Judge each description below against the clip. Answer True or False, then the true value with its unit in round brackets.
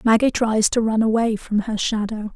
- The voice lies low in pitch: False (220 Hz)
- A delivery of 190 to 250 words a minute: True (205 wpm)